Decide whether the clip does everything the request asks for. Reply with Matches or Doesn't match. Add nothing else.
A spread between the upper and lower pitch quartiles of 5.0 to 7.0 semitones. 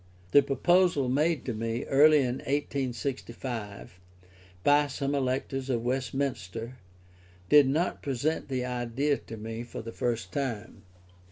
Doesn't match